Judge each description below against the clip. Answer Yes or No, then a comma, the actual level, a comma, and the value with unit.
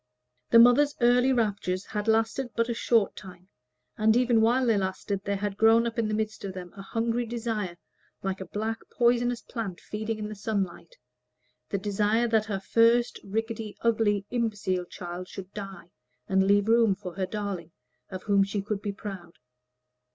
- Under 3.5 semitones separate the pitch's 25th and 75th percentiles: Yes, average, 2.8 semitones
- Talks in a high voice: Yes, high, 210 Hz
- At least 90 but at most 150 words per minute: No, average, 175 wpm